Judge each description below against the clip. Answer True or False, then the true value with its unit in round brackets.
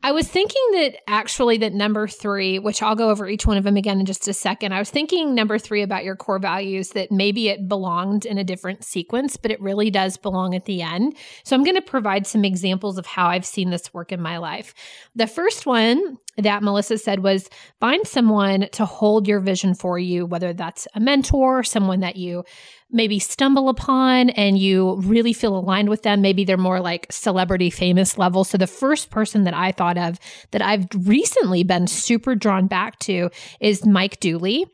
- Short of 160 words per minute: False (205 wpm)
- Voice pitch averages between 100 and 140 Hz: False (200 Hz)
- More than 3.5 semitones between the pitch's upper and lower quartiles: False (3.2 semitones)